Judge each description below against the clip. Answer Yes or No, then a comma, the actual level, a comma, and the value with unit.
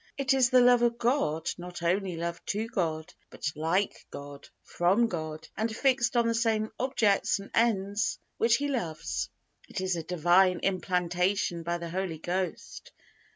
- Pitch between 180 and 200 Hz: Yes, high, 190 Hz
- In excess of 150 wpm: Yes, average, 160 wpm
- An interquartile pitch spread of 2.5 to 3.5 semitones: No, average, 5.2 semitones